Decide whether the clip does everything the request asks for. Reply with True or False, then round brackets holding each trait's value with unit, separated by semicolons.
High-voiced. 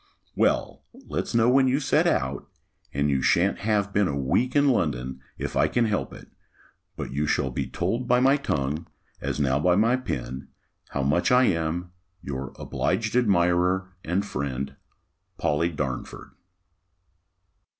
False (90 Hz)